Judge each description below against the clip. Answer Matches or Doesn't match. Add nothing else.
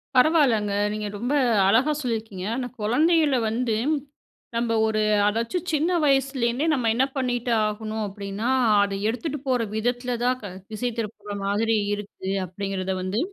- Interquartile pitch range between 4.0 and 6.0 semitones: Doesn't match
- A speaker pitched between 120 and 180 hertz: Doesn't match